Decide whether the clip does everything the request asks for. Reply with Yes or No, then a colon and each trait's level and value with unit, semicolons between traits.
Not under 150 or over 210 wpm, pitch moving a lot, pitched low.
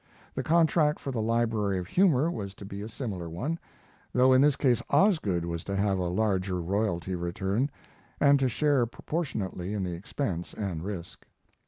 Yes: average, 175 wpm; wide, 6.5 semitones; low, 105 Hz